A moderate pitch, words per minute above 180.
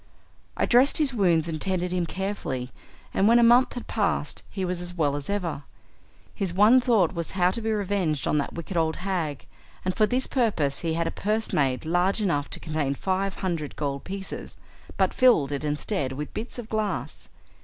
Yes: medium, 180 Hz; average, 195 wpm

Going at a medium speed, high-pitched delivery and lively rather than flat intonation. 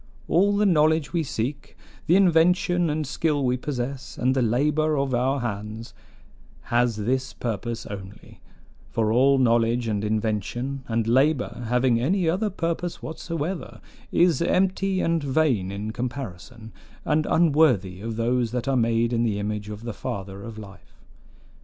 No: average, 150 wpm; low, 125 Hz; wide, 5.7 semitones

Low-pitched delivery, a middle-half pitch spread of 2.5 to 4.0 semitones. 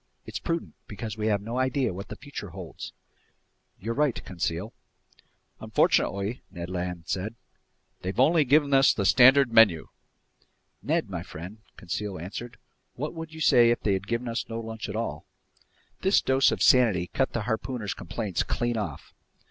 No: low, 115 Hz; average, 5.0 semitones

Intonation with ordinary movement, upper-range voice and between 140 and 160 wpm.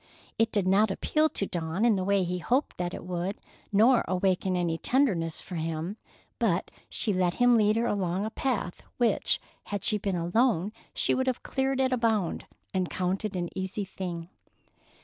No: average, 4.1 semitones; high, 195 Hz; average, 185 wpm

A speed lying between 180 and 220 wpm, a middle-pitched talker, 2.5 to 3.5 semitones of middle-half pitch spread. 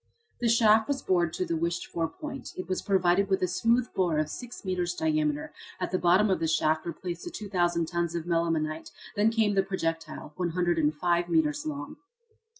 Yes: average, 190 wpm; medium, 175 Hz; average, 2.9 semitones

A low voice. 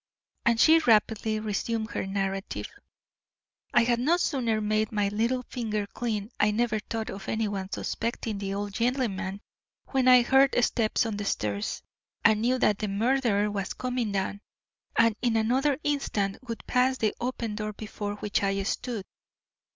No: high, 220 Hz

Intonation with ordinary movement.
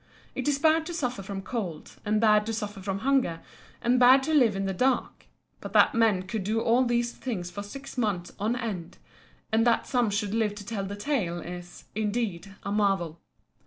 Yes: average, 3.9 semitones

